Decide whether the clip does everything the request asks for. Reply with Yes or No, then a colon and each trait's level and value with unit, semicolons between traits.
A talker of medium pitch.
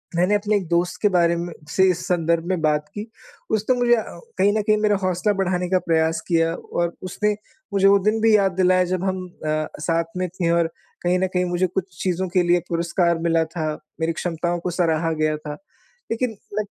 Yes: medium, 180 Hz